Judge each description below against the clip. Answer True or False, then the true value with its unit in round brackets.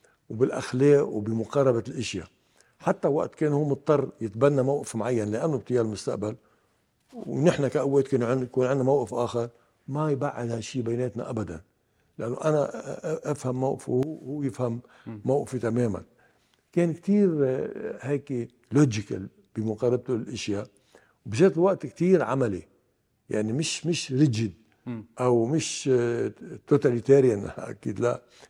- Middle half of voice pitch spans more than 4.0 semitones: False (3.7 semitones)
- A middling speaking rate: False (115 wpm)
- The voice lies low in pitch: True (125 Hz)